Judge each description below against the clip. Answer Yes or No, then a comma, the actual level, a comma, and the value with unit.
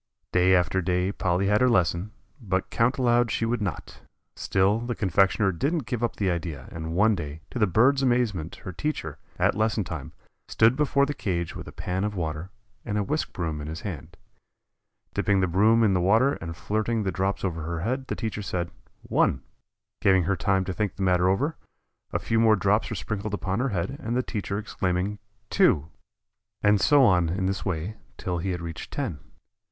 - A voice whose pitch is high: No, low, 100 Hz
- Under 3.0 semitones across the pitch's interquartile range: No, average, 4.1 semitones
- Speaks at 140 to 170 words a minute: No, average, 200 wpm